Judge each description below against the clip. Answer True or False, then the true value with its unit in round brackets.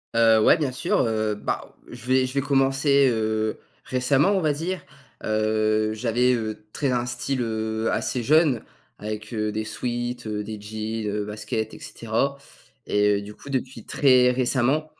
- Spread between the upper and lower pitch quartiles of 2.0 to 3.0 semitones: False (3.5 semitones)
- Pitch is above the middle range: False (115 Hz)